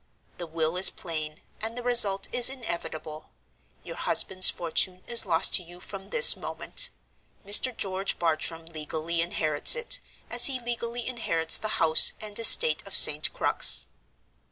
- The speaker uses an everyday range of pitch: No, wide, 6.2 semitones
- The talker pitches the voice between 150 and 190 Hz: Yes, medium, 185 Hz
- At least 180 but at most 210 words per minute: No, average, 150 wpm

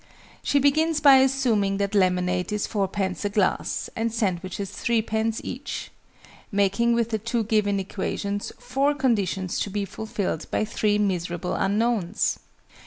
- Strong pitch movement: No, average, 3.2 semitones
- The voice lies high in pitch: Yes, high, 210 Hz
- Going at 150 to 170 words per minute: No, slow, 135 wpm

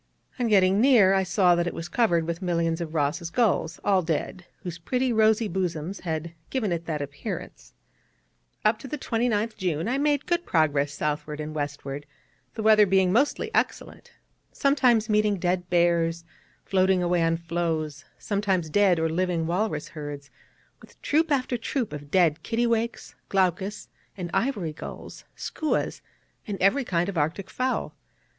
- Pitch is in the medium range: Yes, medium, 180 Hz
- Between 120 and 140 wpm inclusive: No, average, 155 wpm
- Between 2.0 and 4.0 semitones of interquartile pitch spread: No, average, 4.8 semitones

